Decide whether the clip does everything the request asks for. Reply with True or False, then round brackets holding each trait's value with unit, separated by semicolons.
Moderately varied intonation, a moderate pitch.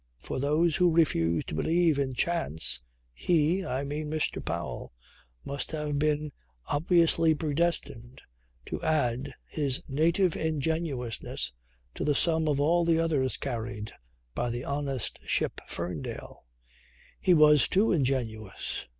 True (4.4 semitones; 150 Hz)